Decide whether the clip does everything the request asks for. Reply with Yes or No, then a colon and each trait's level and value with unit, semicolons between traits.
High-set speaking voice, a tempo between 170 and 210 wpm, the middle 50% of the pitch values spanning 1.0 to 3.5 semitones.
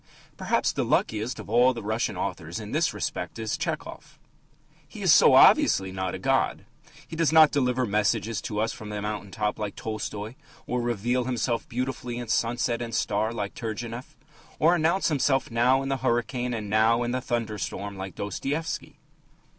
No: low, 115 Hz; average, 175 wpm; average, 2.9 semitones